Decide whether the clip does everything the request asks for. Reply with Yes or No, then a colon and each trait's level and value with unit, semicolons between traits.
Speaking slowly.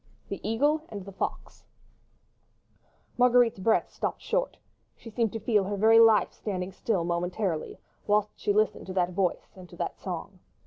No: average, 165 wpm